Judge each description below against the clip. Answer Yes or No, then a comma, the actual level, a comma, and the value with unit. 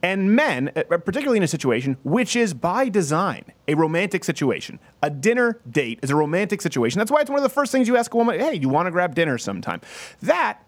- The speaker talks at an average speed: No, fast, 225 wpm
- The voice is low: No, medium, 175 Hz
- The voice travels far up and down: Yes, wide, 7.9 semitones